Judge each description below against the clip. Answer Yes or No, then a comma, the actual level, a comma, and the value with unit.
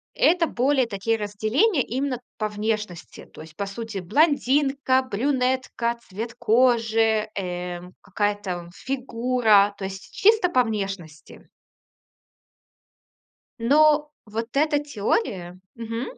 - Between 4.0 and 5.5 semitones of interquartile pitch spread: Yes, average, 4.6 semitones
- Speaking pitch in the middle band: No, high, 225 Hz